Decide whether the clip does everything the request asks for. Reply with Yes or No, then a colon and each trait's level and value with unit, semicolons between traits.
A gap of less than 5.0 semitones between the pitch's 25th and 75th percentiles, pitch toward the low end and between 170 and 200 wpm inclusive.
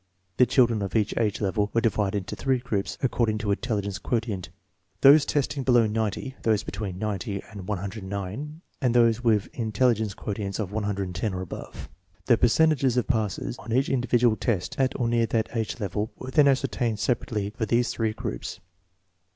Yes: average, 3.2 semitones; low, 110 Hz; average, 185 wpm